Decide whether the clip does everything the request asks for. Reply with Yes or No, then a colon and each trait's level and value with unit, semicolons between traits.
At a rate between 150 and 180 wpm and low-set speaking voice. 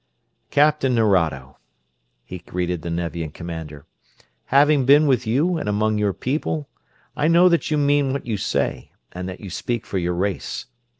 Yes: average, 165 wpm; low, 110 Hz